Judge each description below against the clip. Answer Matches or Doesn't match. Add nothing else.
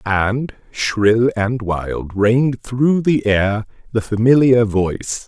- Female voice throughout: Doesn't match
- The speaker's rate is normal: Doesn't match